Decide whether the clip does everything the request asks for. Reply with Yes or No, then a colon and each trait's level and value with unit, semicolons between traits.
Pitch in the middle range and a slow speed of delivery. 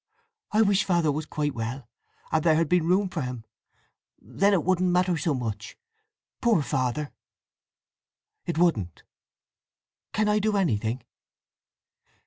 Yes: medium, 160 Hz; slow, 130 wpm